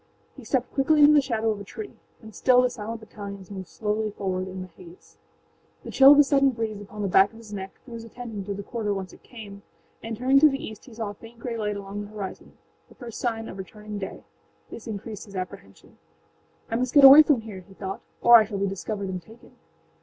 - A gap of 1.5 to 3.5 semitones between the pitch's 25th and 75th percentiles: Yes, average, 3.2 semitones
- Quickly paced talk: Yes, fast, 235 wpm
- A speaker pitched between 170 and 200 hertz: No, high, 215 Hz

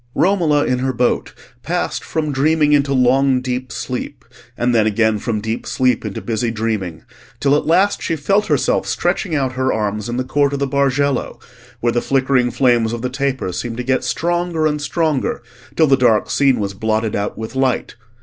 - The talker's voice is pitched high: No, low, 130 Hz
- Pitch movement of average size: Yes, average, 3.8 semitones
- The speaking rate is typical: Yes, average, 190 wpm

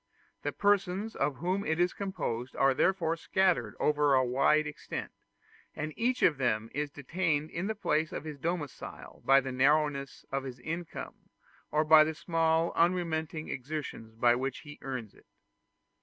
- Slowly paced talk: No, average, 160 wpm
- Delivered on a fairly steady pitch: No, average, 3.9 semitones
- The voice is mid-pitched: Yes, medium, 155 Hz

